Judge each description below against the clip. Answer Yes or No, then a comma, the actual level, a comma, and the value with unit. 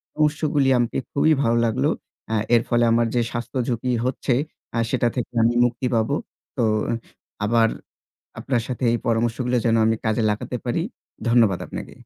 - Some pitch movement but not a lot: No, narrow, 1.9 semitones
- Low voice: Yes, low, 120 Hz